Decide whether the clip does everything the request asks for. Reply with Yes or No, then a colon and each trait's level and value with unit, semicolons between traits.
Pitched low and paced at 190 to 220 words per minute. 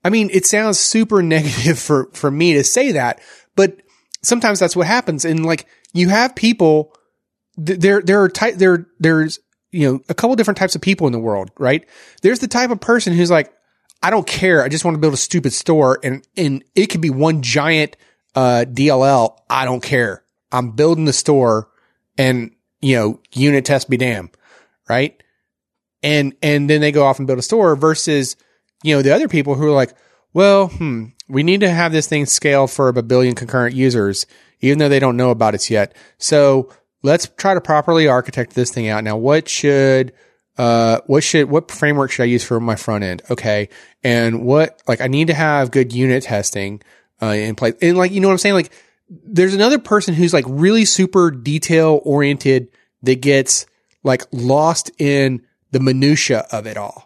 No: medium, 145 Hz; average, 200 wpm